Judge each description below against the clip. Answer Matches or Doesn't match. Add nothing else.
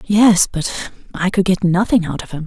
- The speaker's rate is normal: Doesn't match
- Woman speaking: Matches